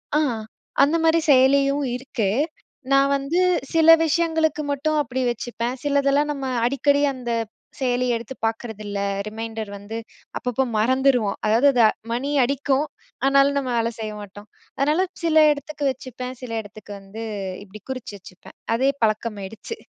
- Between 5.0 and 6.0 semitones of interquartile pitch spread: No, average, 4.1 semitones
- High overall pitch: Yes, very high, 260 Hz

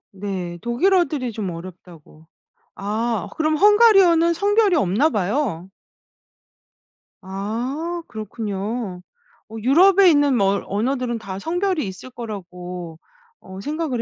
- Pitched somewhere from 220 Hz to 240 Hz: Yes, high, 230 Hz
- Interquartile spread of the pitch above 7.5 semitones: Yes, wide, 8.7 semitones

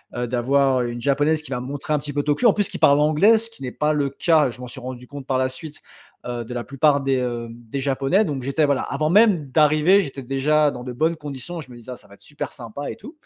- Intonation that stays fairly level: No, average, 3.3 semitones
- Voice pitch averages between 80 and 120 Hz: No, medium, 140 Hz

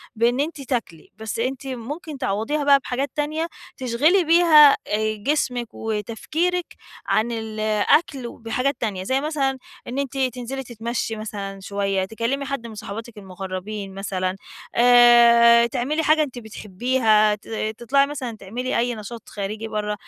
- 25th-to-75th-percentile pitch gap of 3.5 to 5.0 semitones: Yes, average, 4.2 semitones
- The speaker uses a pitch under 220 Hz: No, high, 235 Hz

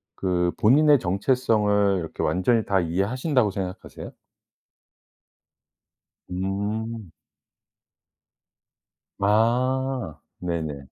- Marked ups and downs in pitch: No, average, 4.7 semitones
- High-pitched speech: No, low, 100 Hz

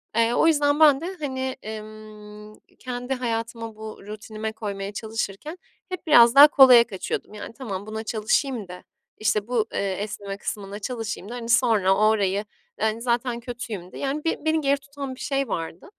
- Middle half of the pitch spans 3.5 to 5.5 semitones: Yes, average, 3.9 semitones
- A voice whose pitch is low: No, high, 230 Hz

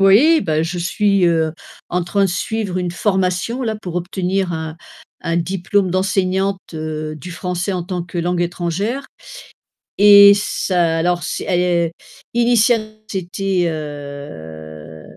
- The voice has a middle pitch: Yes, medium, 180 Hz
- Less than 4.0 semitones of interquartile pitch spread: Yes, average, 2.9 semitones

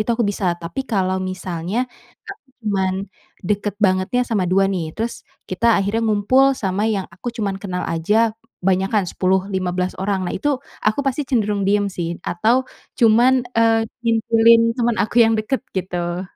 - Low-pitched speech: No, high, 205 Hz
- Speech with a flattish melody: No, average, 3.6 semitones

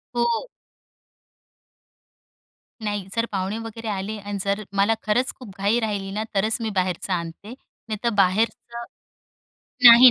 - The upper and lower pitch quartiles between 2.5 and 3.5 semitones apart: Yes, average, 2.8 semitones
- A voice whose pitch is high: Yes, high, 210 Hz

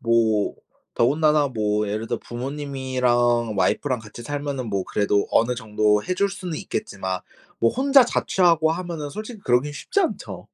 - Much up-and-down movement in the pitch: Yes, wide, 6.2 semitones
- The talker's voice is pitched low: Yes, low, 130 Hz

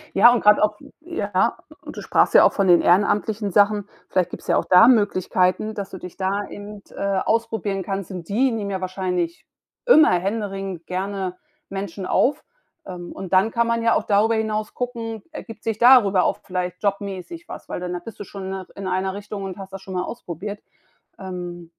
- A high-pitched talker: Yes, high, 200 Hz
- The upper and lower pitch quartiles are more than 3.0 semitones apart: No, average, 2.7 semitones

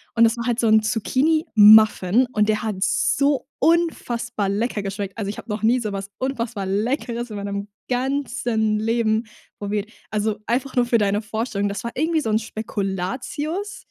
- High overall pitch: Yes, high, 220 Hz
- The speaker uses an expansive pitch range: No, average, 3.3 semitones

